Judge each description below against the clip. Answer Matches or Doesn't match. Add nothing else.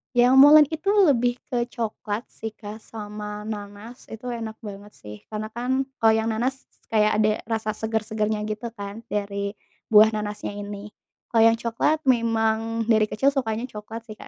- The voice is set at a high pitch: Matches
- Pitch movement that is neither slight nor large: Doesn't match